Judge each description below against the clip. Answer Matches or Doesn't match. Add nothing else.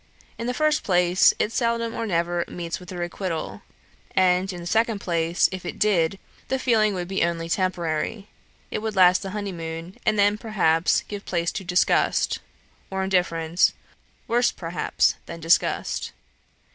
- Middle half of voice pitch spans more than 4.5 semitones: Doesn't match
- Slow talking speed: Doesn't match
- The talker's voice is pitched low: Doesn't match